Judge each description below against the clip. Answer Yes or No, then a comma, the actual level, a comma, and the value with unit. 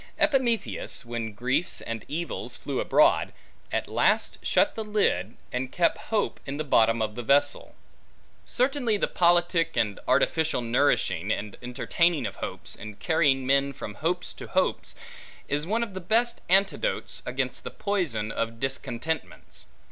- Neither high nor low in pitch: Yes, medium, 145 Hz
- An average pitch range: No, wide, 8.4 semitones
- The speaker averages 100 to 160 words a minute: Yes, average, 150 wpm